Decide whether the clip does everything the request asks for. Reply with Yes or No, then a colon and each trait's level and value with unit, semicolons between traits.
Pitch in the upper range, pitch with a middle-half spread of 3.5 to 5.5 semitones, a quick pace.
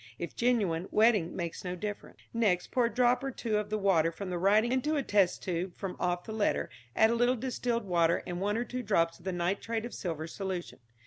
Yes: high, 200 Hz; average, 4.8 semitones; fast, 230 wpm